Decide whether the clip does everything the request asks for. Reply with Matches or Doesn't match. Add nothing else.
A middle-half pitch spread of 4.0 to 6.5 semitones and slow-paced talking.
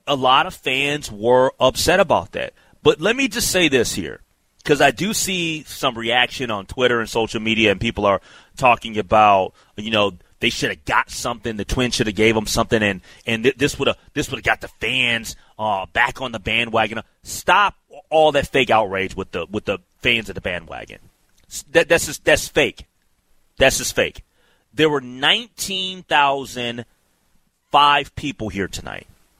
Doesn't match